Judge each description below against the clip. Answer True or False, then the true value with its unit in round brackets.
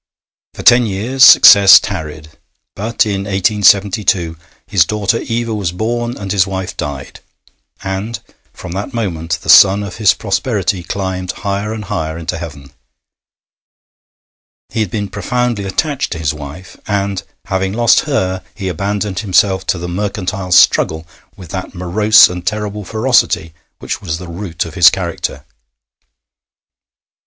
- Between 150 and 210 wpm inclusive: False (140 wpm)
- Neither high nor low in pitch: False (100 Hz)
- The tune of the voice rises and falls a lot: False (3.0 semitones)